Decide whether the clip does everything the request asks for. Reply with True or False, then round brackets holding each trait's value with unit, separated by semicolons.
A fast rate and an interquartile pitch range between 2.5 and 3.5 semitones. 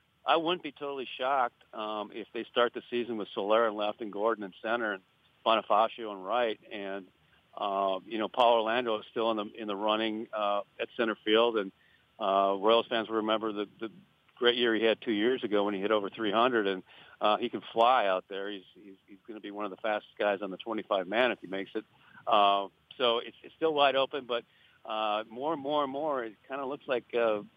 True (230 wpm; 2.8 semitones)